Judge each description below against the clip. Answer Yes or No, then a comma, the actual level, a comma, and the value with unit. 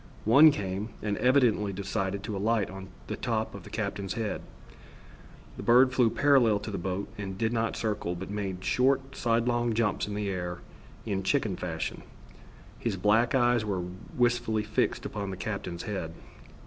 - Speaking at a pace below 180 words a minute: Yes, average, 165 wpm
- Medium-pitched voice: No, low, 105 Hz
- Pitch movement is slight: No, average, 3.4 semitones